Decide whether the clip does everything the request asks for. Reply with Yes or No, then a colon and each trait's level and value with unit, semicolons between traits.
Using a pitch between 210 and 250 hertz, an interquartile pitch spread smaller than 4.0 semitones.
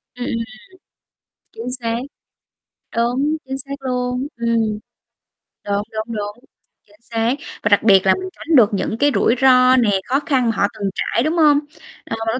Yes: high, 240 Hz; average, 3.4 semitones